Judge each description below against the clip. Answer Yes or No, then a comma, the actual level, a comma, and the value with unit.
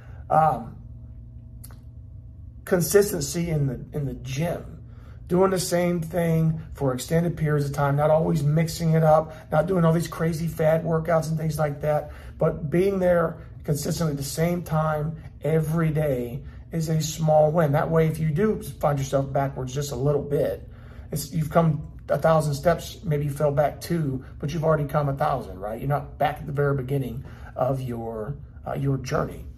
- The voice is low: No, medium, 155 Hz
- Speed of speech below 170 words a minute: No, average, 180 wpm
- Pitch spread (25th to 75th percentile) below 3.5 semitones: Yes, average, 2.8 semitones